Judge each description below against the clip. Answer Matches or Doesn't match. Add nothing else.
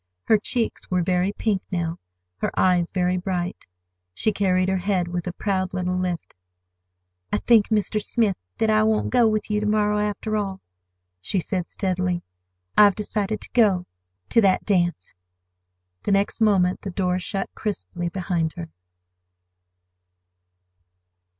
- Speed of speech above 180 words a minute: Doesn't match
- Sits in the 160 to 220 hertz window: Matches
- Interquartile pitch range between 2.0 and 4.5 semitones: Matches